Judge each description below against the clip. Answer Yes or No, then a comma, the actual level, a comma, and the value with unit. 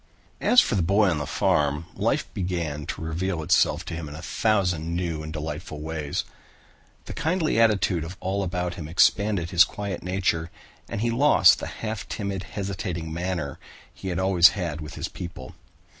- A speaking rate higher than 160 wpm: Yes, average, 175 wpm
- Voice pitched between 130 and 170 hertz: No, very low, 90 Hz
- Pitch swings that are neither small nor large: Yes, average, 3.5 semitones